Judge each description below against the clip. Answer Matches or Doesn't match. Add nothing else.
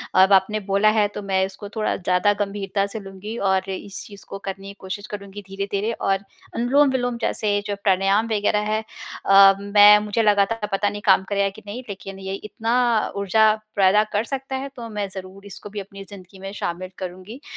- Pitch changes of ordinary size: Doesn't match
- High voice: Matches